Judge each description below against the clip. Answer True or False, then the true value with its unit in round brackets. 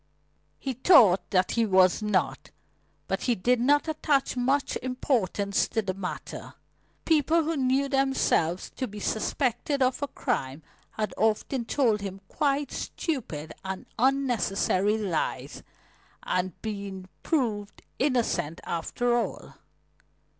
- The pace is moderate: False (120 wpm)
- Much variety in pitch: True (5.7 semitones)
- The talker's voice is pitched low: False (235 Hz)